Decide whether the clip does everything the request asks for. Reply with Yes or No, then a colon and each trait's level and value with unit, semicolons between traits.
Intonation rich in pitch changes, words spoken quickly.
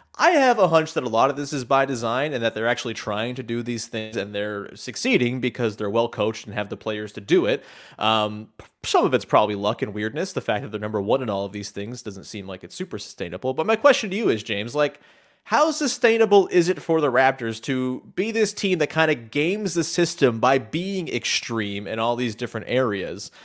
Yes: wide, 7.1 semitones; fast, 235 wpm